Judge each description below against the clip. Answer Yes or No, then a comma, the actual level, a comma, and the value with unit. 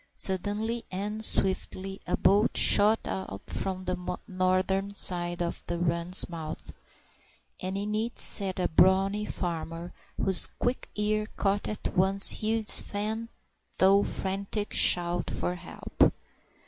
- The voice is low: No, high, 190 Hz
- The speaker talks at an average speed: No, slow, 125 wpm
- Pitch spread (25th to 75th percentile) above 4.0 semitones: No, average, 2.7 semitones